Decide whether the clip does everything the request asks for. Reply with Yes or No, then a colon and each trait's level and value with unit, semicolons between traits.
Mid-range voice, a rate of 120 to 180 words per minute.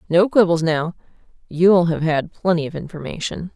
Yes: medium, 170 Hz; slow, 135 wpm